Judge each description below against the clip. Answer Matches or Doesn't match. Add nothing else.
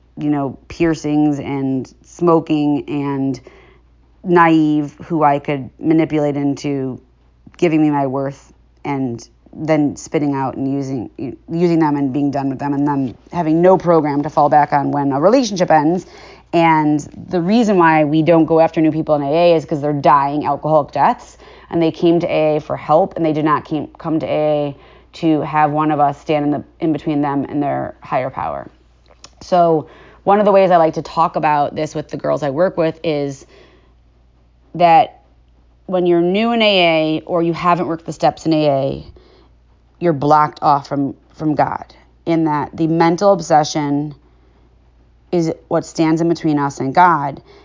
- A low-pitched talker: Doesn't match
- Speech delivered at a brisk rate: Doesn't match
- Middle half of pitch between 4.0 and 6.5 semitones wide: Doesn't match